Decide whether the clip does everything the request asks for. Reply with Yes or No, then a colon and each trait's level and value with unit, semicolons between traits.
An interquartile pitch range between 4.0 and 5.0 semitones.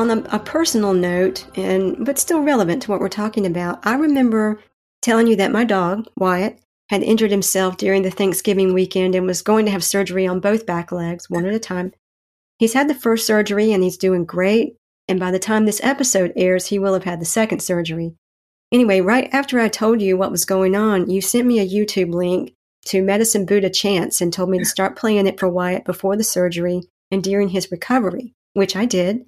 No: average, 3.0 semitones